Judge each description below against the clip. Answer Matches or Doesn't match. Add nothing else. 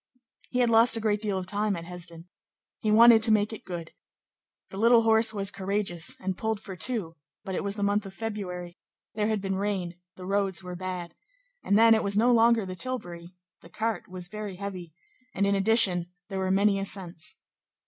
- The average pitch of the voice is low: Doesn't match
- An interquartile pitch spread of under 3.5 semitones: Matches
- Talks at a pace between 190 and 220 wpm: Matches